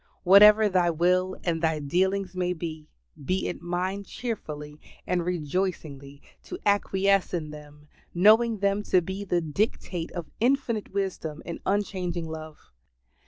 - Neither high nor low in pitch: Yes, medium, 180 Hz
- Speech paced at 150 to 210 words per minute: No, slow, 135 wpm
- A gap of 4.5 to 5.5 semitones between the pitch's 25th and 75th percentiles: No, average, 3.7 semitones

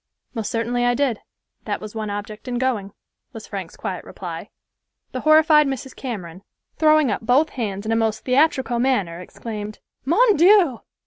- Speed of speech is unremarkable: Yes, average, 165 wpm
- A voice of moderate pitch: No, high, 245 Hz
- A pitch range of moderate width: Yes, average, 4.8 semitones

